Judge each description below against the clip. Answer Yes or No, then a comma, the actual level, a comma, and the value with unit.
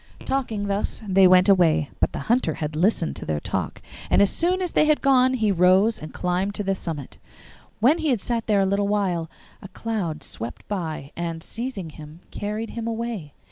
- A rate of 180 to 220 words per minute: Yes, average, 200 wpm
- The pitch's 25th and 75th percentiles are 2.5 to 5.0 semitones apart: No, wide, 5.5 semitones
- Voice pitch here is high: Yes, high, 195 Hz